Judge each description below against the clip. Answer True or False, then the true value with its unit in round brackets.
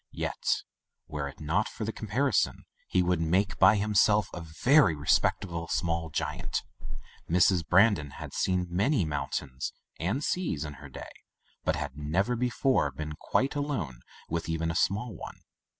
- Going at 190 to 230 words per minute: False (155 wpm)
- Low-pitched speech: True (90 Hz)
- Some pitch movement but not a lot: False (5.7 semitones)